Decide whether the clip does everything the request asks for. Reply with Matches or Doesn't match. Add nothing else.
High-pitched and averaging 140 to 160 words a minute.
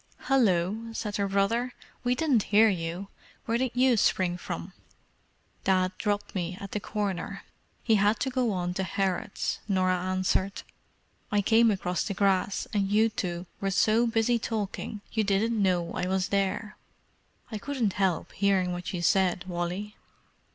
Matches